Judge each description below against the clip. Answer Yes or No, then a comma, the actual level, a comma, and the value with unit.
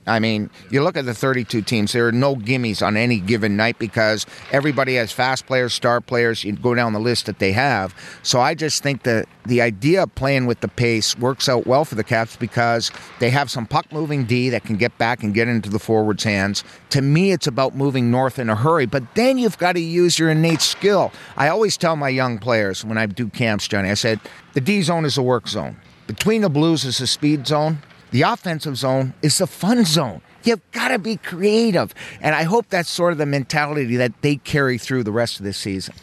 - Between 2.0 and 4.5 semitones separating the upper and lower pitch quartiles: No, average, 5.1 semitones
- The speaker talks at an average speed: No, fast, 235 wpm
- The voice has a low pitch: Yes, low, 130 Hz